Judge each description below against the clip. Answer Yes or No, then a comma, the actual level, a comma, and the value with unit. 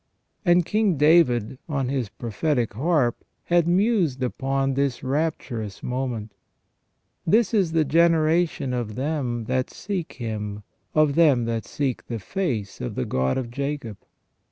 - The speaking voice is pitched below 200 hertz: Yes, low, 135 Hz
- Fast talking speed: No, average, 145 wpm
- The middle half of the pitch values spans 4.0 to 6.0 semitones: Yes, wide, 5.4 semitones